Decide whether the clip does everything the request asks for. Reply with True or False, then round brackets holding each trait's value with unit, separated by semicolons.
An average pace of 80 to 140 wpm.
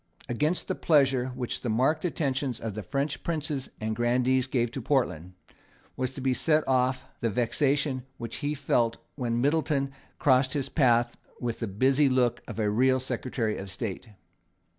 False (165 wpm)